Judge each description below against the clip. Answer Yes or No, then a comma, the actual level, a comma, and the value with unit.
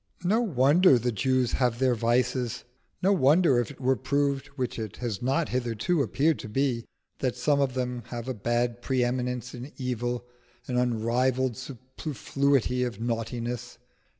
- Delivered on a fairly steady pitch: Yes, narrow, 2.1 semitones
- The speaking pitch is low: Yes, low, 125 Hz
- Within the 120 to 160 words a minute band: Yes, average, 155 wpm